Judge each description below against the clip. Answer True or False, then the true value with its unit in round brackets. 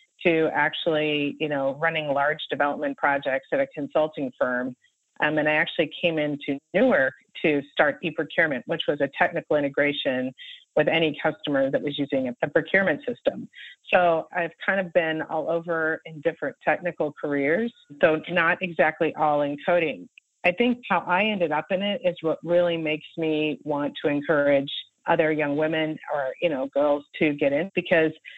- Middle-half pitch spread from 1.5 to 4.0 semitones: True (3.1 semitones)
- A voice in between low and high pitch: True (160 Hz)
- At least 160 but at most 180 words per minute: True (170 wpm)